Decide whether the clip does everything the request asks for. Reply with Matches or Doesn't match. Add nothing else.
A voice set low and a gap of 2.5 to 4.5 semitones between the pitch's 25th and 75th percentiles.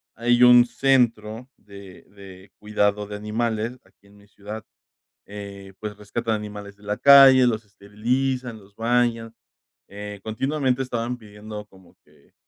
Matches